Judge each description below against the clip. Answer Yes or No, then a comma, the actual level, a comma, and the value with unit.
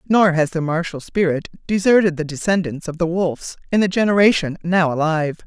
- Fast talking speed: No, average, 175 wpm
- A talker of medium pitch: Yes, medium, 170 Hz